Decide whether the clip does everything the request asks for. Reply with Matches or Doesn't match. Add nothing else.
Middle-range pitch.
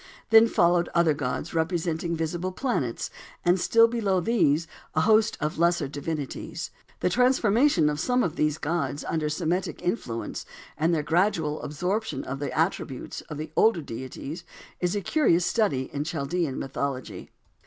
Matches